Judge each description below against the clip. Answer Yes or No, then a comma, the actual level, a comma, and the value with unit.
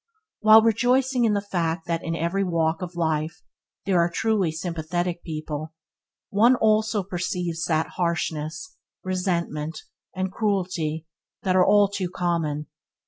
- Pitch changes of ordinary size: Yes, average, 3.8 semitones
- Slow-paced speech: Yes, slow, 130 wpm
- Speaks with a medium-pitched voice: Yes, medium, 175 Hz